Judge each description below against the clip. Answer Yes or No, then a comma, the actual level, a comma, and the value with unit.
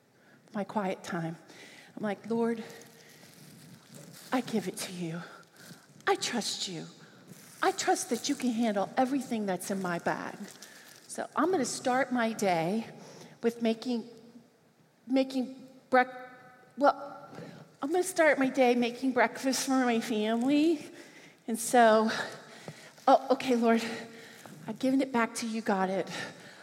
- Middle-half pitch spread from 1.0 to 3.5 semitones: No, average, 3.9 semitones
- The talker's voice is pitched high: Yes, high, 230 Hz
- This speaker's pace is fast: No, slow, 135 wpm